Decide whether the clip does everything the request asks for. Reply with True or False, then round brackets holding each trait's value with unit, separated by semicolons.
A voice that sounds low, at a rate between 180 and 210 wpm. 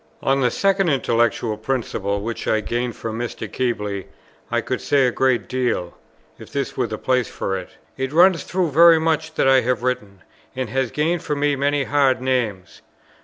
True (130 Hz; 185 wpm)